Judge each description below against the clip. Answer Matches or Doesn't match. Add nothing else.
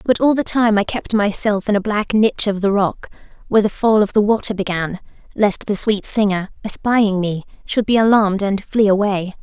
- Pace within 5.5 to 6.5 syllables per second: Doesn't match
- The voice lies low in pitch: Doesn't match